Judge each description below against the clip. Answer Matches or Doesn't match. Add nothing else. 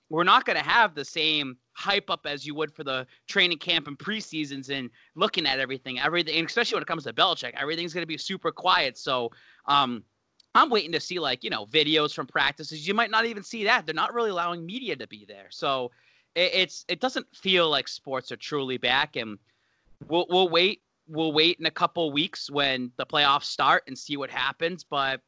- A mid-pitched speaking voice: Matches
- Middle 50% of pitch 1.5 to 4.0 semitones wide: Doesn't match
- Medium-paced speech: Doesn't match